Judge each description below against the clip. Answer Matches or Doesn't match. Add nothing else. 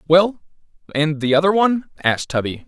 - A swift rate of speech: Doesn't match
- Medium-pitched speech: Matches